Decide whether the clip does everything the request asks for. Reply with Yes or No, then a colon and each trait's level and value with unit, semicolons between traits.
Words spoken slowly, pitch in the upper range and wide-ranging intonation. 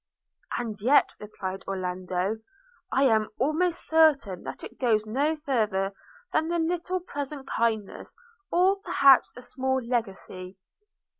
Yes: slow, 125 wpm; very high, 250 Hz; wide, 6.8 semitones